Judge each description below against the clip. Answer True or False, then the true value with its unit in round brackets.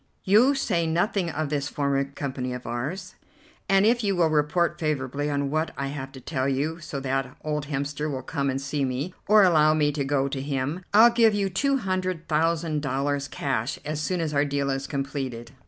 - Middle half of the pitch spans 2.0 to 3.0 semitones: False (3.8 semitones)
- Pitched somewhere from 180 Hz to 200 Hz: False (150 Hz)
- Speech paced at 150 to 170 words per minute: False (205 wpm)